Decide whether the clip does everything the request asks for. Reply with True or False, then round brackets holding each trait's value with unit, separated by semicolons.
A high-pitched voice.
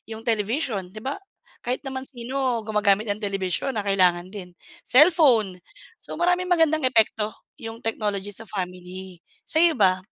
True (220 Hz)